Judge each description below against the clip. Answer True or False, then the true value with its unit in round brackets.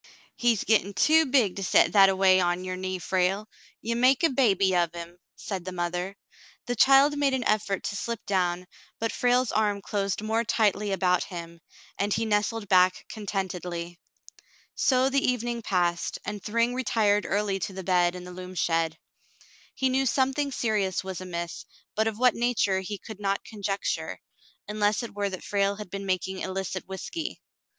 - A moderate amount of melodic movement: True (3.6 semitones)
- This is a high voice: True (200 Hz)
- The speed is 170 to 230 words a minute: True (180 wpm)